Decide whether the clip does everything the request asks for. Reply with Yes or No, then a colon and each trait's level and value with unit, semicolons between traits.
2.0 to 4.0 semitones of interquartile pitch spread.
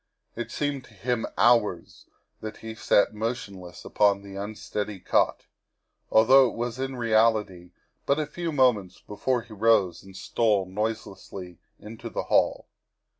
Yes: average, 3.4 semitones